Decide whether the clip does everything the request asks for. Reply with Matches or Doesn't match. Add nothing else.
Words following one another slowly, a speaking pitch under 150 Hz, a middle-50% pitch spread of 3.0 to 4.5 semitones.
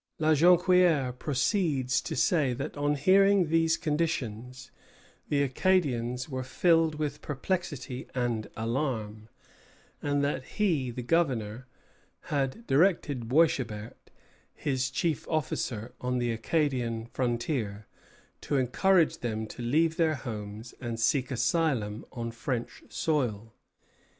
Doesn't match